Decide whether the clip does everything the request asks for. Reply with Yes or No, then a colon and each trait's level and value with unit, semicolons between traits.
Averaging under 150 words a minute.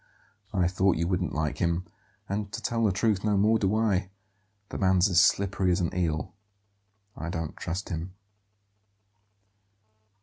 No: average, 155 wpm